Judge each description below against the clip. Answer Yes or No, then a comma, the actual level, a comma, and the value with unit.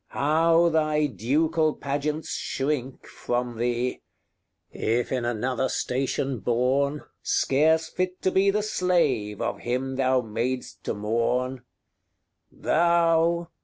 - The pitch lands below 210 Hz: Yes, low, 135 Hz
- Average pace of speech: No, slow, 115 wpm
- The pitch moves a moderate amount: Yes, average, 4.7 semitones